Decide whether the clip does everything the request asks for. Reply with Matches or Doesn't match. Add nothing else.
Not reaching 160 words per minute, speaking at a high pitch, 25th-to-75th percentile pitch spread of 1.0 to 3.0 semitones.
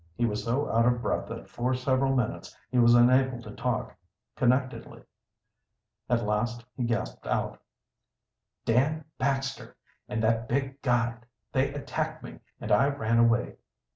Doesn't match